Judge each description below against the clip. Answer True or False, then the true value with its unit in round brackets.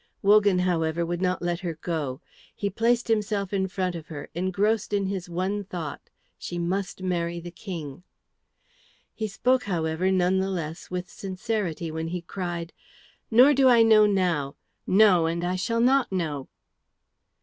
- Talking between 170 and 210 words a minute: False (160 wpm)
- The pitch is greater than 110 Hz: True (185 Hz)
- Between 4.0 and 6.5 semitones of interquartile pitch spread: False (3.2 semitones)